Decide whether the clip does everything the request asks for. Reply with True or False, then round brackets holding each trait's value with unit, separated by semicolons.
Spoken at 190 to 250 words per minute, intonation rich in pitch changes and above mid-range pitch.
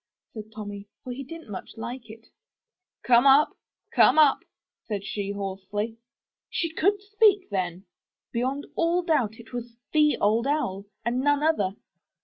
False (145 wpm; 6.8 semitones; 240 Hz)